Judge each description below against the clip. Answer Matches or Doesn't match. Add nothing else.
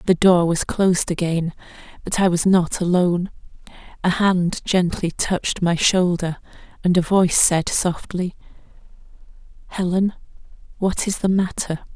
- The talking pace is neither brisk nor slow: Doesn't match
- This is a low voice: Doesn't match